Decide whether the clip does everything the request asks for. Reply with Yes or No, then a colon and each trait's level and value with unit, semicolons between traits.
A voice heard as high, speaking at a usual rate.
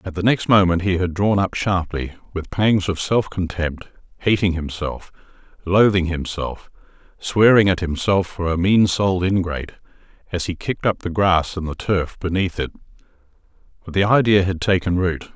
No: very low, 90 Hz; average, 170 wpm